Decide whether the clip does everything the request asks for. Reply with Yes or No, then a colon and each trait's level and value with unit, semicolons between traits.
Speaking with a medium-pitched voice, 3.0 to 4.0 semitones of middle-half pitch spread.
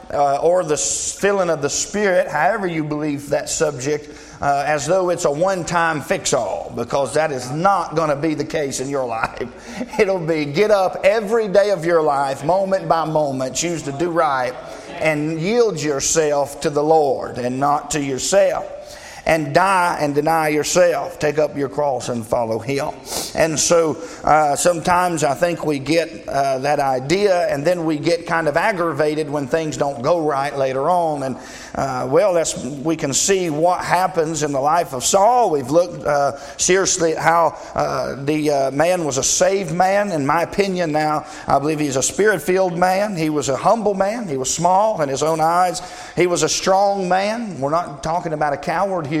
Yes: medium, 160 Hz; average, 3.7 semitones